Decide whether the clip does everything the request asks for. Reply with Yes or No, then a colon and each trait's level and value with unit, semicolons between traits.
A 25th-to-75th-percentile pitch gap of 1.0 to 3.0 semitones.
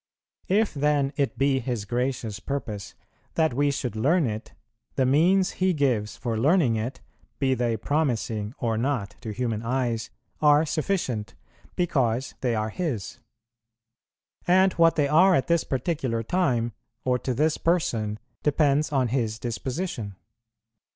No: average, 5.1 semitones